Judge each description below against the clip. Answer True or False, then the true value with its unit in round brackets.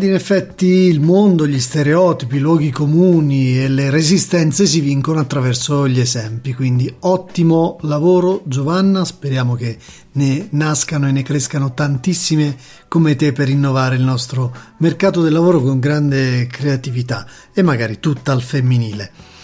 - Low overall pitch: False (145 Hz)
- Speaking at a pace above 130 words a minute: True (140 wpm)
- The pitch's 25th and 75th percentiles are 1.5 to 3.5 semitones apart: False (4.1 semitones)